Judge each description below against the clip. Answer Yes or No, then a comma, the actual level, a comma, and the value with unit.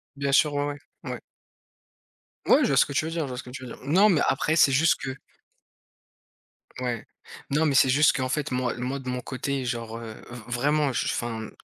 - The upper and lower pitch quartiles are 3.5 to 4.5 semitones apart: No, average, 2.9 semitones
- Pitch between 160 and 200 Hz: No, low, 135 Hz